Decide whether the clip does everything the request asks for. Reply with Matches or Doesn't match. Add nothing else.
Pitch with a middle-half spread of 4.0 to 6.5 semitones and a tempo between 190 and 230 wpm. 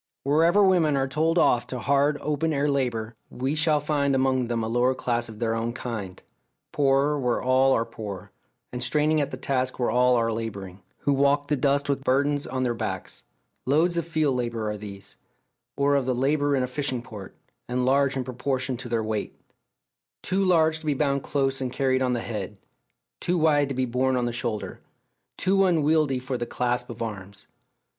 Doesn't match